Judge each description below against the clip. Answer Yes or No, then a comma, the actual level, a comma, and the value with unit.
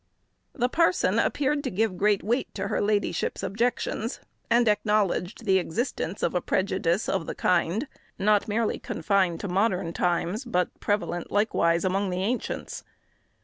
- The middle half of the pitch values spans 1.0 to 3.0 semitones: No, average, 3.7 semitones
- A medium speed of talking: Yes, average, 145 wpm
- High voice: Yes, high, 205 Hz